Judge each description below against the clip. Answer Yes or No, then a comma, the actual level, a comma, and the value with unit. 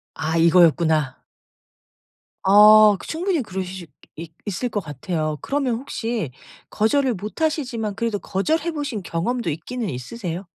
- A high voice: Yes, high, 205 Hz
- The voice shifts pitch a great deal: Yes, wide, 6.7 semitones